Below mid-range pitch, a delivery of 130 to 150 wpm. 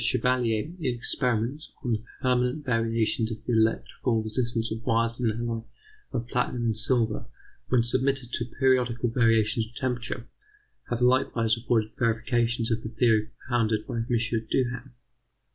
Yes: low, 120 Hz; average, 145 wpm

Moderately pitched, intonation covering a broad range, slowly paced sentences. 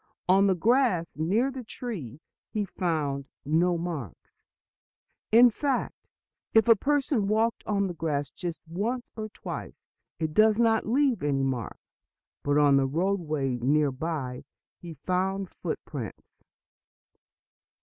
Yes: medium, 180 Hz; wide, 7.0 semitones; slow, 130 wpm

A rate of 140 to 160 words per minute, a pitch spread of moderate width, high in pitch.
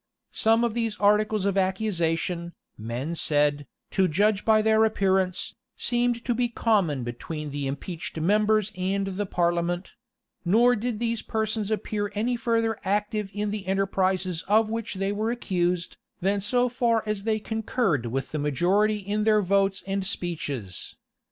Yes: average, 150 wpm; average, 3.7 semitones; high, 200 Hz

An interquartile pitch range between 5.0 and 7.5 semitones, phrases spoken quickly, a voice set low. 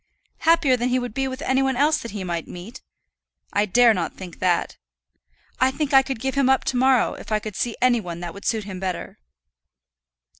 No: average, 5.3 semitones; fast, 220 wpm; high, 245 Hz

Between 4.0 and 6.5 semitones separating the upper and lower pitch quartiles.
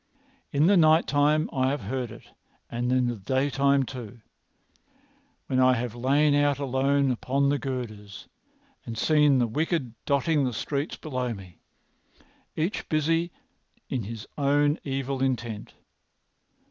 No: average, 2.9 semitones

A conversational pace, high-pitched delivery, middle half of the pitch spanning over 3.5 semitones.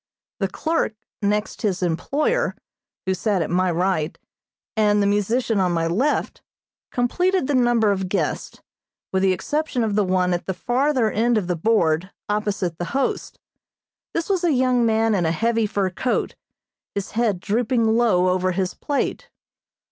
Yes: average, 165 wpm; high, 210 Hz; average, 4.7 semitones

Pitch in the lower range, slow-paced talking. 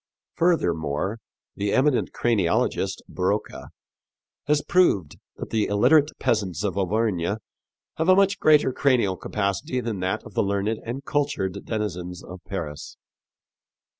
Yes: low, 105 Hz; slow, 125 wpm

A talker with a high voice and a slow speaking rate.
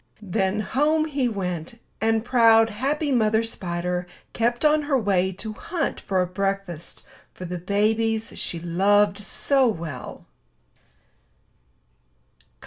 Yes: high, 215 Hz; slow, 120 wpm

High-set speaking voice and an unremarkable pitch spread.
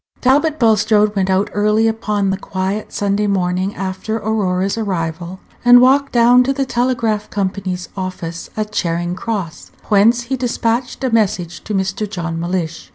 Yes: high, 205 Hz; average, 3.5 semitones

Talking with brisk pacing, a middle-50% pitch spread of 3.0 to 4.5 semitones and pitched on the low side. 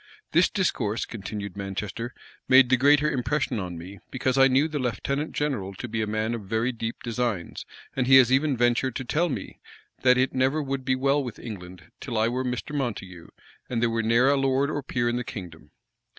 Yes: fast, 210 wpm; average, 3.7 semitones; low, 125 Hz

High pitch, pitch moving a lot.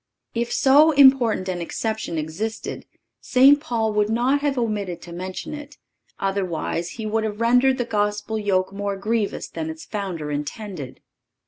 No: high, 210 Hz; average, 4.3 semitones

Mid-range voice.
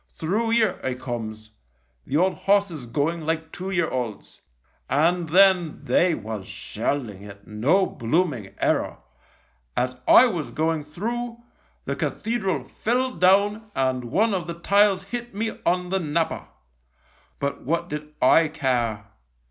Yes: medium, 165 Hz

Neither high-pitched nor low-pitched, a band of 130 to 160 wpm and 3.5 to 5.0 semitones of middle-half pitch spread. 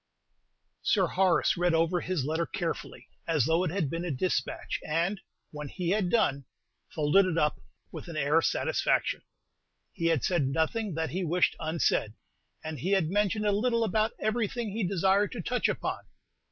No: medium, 175 Hz; average, 175 wpm; average, 3.9 semitones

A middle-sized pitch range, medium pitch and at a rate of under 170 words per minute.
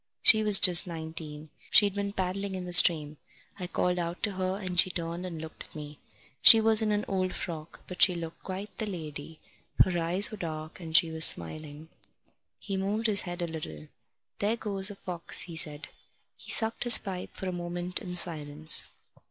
No: average, 3.4 semitones; medium, 180 Hz; average, 195 wpm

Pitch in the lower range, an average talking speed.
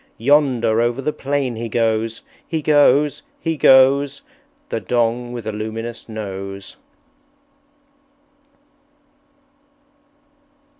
No: low, 120 Hz; slow, 90 wpm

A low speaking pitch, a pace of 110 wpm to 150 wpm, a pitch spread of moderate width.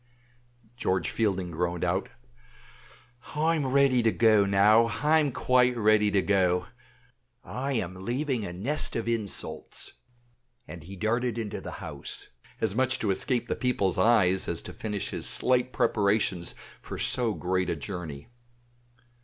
Yes: low, 110 Hz; average, 140 wpm; average, 4.9 semitones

